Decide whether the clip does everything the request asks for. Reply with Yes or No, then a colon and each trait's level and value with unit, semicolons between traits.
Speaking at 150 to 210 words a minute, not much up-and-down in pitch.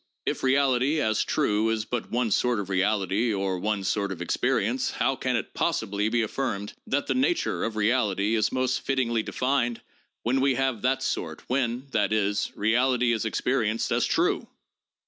No: average, 170 wpm; average, 3.7 semitones